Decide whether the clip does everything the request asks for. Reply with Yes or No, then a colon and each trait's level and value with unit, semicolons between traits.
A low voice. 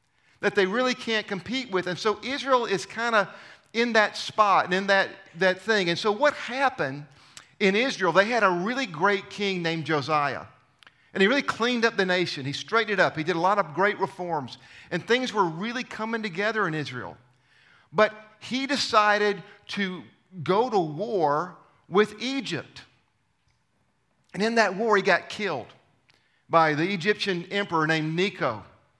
No: high, 200 Hz